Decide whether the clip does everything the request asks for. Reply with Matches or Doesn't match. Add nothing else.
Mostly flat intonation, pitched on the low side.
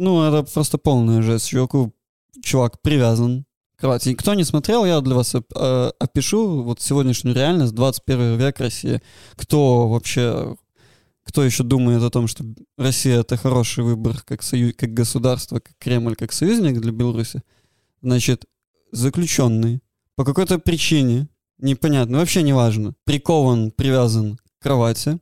Doesn't match